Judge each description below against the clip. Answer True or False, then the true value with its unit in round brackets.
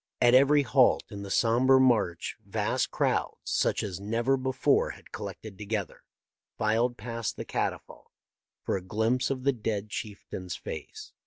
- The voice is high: False (115 Hz)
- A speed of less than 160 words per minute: True (150 wpm)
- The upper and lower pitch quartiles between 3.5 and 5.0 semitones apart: True (3.9 semitones)